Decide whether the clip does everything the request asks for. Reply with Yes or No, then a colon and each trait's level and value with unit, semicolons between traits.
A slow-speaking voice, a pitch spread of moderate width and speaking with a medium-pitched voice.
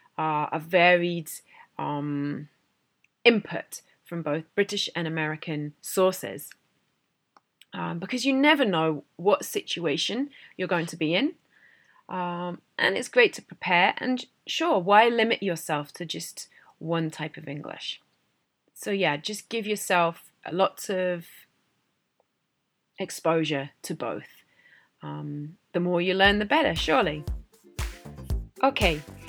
Yes: slow, 120 wpm; average, 5.0 semitones; medium, 175 Hz